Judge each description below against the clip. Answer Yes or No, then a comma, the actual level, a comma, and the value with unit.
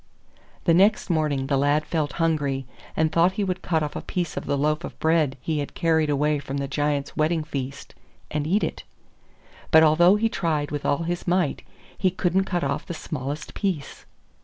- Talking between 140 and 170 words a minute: No, average, 185 wpm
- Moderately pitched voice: Yes, medium, 155 Hz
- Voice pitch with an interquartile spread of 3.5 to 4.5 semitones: No, average, 3.1 semitones